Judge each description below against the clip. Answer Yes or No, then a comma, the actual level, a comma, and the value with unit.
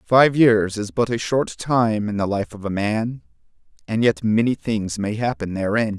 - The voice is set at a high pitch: No, low, 110 Hz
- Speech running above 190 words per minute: Yes, average, 200 wpm